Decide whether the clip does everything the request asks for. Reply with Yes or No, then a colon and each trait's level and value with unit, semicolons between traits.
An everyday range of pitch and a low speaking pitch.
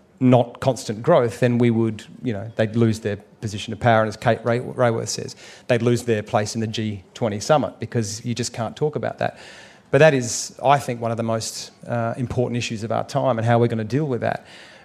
No: narrow, 1.9 semitones; low, 120 Hz